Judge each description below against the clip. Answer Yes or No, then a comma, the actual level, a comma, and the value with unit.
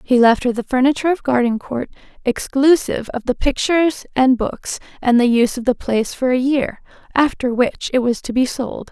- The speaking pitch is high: Yes, very high, 255 Hz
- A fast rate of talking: No, average, 195 wpm